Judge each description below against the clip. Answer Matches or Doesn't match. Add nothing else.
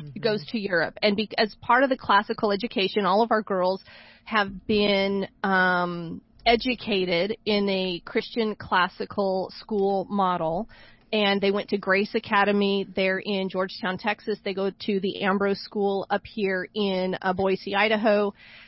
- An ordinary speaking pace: Matches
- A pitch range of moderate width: Doesn't match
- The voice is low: Doesn't match